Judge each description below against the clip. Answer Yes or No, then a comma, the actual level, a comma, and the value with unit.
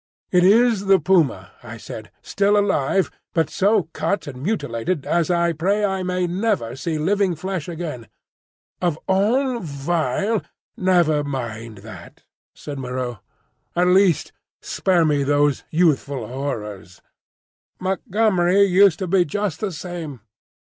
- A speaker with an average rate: No, slow, 130 wpm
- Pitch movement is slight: No, average, 5.2 semitones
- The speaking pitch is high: No, medium, 175 Hz